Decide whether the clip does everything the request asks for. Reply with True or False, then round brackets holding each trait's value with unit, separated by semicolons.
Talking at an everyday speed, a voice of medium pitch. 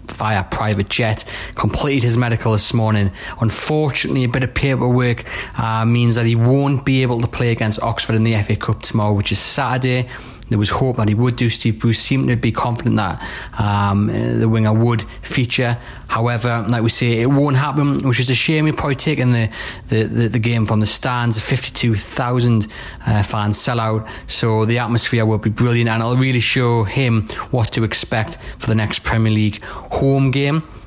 False (195 wpm; 115 Hz)